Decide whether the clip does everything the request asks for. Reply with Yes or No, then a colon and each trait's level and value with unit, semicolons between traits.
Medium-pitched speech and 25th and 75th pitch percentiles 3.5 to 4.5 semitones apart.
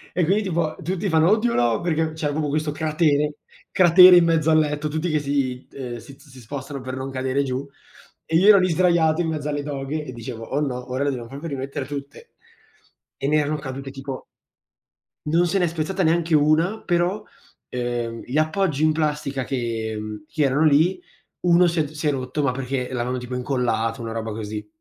Yes: medium, 145 Hz; average, 3.8 semitones